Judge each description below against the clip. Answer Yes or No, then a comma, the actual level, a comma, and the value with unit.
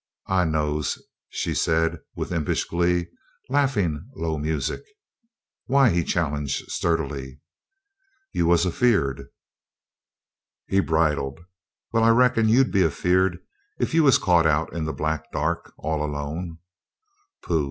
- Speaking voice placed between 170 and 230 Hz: No, very low, 85 Hz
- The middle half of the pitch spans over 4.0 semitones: No, average, 3.7 semitones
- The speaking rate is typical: No, slow, 130 wpm